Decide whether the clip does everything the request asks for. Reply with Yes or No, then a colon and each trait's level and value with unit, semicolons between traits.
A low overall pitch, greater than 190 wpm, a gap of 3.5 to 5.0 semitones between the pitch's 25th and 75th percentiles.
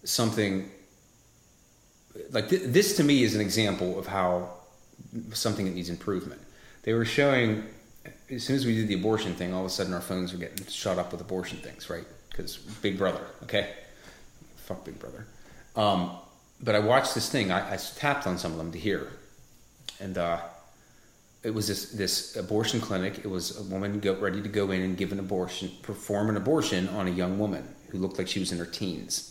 No: very low, 95 Hz; average, 200 wpm; average, 3.1 semitones